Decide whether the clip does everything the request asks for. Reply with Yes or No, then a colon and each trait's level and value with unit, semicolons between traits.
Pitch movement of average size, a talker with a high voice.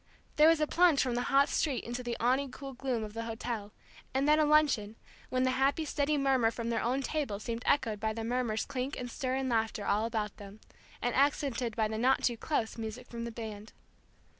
Yes: average, 3.5 semitones; high, 245 Hz